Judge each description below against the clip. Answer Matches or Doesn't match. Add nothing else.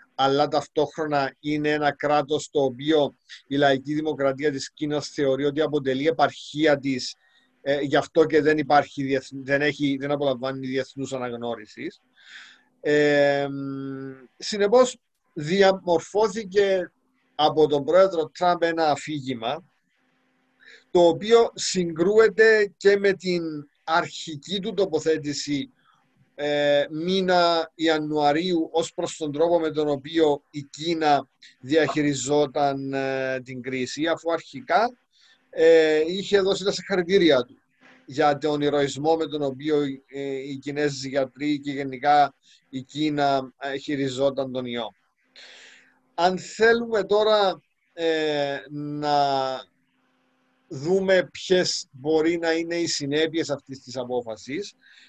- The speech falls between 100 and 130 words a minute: Matches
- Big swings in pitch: Doesn't match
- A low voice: Doesn't match